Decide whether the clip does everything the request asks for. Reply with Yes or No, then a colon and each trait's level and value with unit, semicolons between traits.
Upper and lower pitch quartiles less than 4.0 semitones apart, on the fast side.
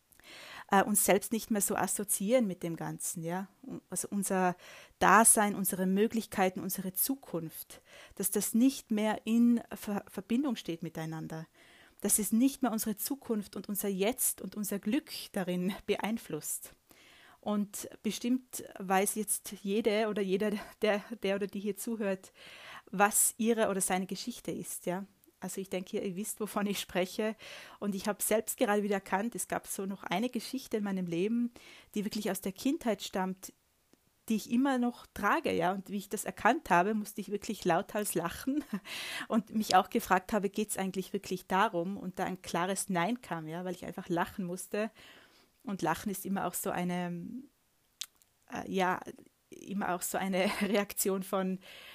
No: average, 2.8 semitones; average, 165 wpm